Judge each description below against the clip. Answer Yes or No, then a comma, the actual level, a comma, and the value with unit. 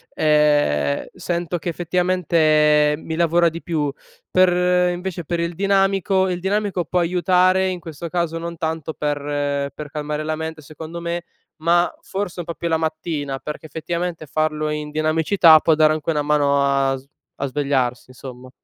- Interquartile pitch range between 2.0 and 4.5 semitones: Yes, average, 2.7 semitones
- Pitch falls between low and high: Yes, medium, 160 Hz